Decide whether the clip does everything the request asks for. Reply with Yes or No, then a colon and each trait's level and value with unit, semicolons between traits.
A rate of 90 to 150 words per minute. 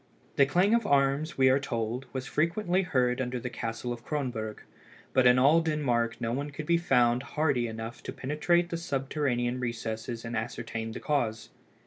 No: average, 175 wpm